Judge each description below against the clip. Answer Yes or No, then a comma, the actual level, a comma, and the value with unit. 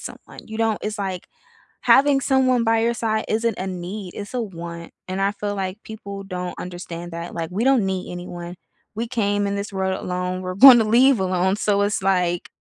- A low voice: No, high, 200 Hz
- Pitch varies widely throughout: No, average, 3.4 semitones